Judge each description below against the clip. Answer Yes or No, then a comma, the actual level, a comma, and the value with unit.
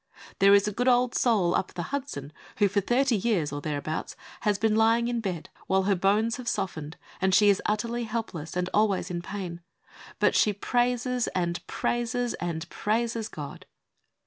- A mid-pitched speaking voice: No, high, 205 Hz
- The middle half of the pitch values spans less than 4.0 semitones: No, average, 4.7 semitones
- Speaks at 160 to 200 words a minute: Yes, average, 175 wpm